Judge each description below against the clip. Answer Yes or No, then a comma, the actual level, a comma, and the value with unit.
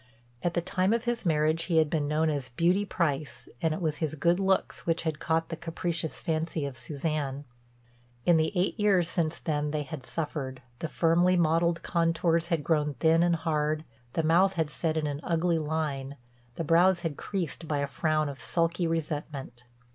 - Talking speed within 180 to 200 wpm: Yes, average, 190 wpm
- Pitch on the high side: No, medium, 160 Hz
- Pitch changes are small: Yes, narrow, 2.2 semitones